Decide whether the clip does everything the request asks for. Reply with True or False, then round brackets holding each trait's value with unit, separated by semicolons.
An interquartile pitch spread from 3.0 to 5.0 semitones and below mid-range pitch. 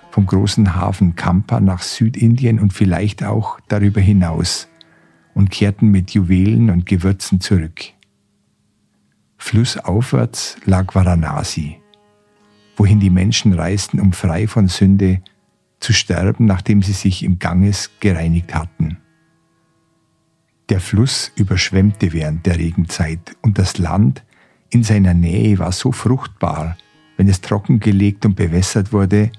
False (2.4 semitones; 100 Hz)